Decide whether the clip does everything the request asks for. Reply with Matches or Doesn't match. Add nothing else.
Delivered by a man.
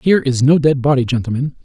Matches